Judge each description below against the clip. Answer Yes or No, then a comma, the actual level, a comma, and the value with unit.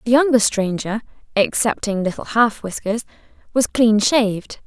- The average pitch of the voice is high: Yes, high, 225 Hz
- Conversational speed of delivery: No, slow, 130 wpm